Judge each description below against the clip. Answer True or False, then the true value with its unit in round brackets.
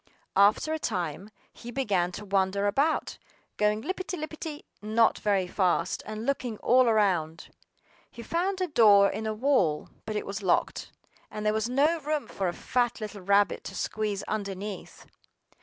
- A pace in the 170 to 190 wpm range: False (160 wpm)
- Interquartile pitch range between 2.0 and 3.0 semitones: False (4.4 semitones)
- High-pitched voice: True (215 Hz)